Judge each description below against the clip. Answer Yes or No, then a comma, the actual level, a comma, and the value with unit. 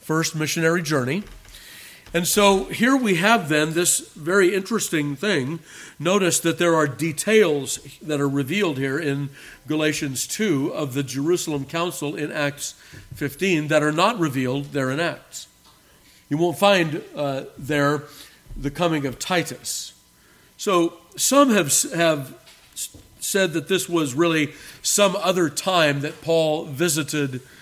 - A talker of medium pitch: Yes, medium, 155 Hz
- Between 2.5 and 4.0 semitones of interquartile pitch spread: Yes, average, 3.6 semitones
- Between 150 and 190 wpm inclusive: No, slow, 135 wpm